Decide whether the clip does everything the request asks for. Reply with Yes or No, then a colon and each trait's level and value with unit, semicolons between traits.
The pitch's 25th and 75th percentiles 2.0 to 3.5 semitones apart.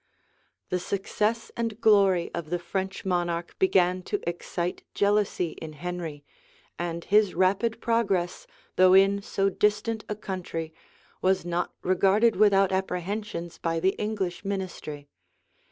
Yes: average, 2.9 semitones